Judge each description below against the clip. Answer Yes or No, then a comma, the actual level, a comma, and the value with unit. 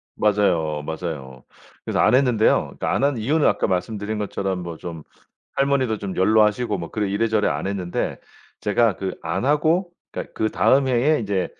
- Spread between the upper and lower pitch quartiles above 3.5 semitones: Yes, average, 5.1 semitones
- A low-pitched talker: Yes, low, 105 Hz